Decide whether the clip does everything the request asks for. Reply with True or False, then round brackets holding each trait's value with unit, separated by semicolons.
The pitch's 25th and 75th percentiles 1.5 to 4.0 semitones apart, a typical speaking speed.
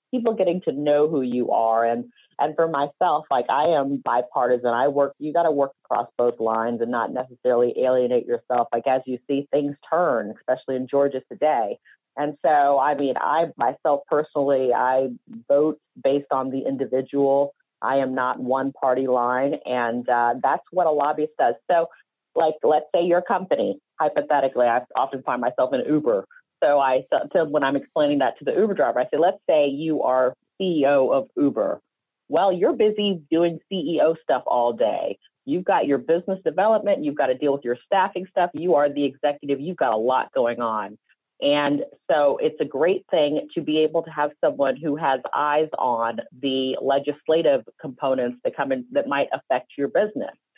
False (4.7 semitones; 185 wpm)